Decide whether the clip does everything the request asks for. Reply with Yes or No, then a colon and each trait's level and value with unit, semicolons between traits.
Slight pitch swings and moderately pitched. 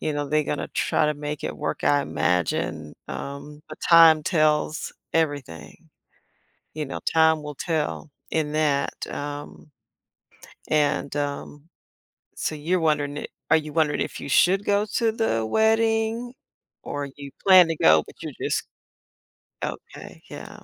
Yes: narrow, 2.3 semitones; medium, 150 Hz